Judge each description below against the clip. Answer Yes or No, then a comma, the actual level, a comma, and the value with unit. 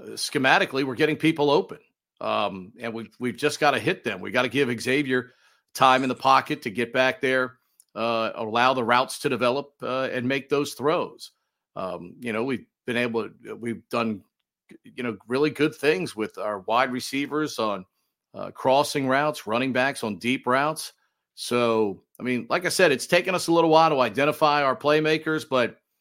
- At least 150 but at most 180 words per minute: No, average, 190 wpm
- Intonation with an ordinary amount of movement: Yes, average, 3.6 semitones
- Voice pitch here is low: Yes, low, 130 Hz